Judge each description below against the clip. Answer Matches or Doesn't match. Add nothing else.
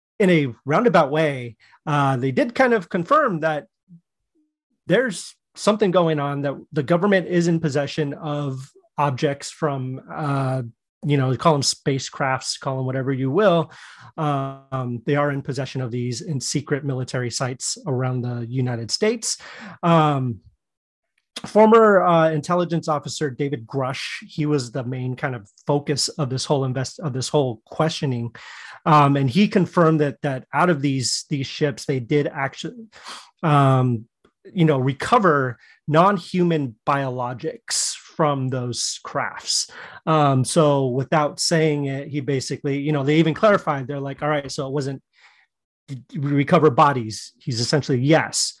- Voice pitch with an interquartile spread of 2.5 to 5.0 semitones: Matches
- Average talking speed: Matches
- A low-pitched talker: Doesn't match